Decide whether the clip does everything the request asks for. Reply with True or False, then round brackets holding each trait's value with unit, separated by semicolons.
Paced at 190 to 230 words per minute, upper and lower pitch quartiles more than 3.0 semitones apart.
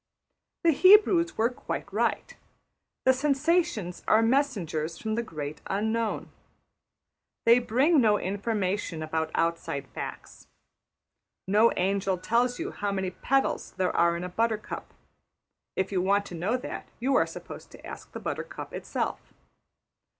False (135 wpm; 5.3 semitones)